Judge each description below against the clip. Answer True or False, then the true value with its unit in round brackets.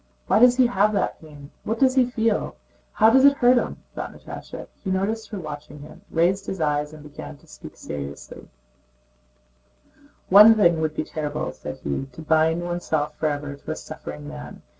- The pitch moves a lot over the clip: True (6.6 semitones)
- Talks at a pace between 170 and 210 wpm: True (180 wpm)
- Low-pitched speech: False (160 Hz)